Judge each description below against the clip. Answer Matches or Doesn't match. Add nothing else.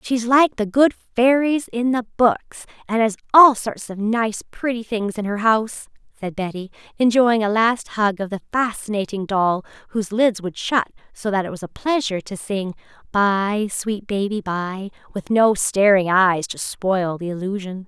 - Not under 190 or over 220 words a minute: Doesn't match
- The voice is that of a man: Doesn't match